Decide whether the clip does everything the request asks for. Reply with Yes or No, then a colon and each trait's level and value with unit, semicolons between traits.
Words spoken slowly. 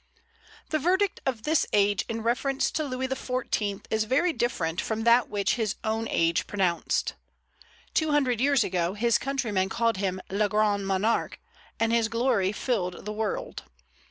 No: average, 155 wpm